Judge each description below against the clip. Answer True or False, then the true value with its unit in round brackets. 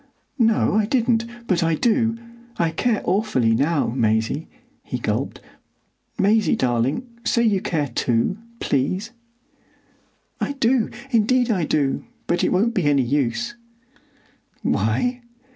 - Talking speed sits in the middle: False (115 wpm)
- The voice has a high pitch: True (200 Hz)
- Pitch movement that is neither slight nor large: False (8.4 semitones)